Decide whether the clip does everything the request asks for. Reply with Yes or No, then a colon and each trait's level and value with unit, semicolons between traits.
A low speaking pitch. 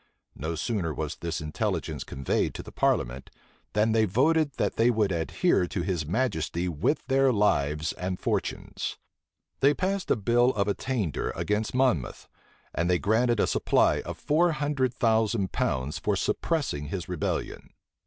Yes: low, 105 Hz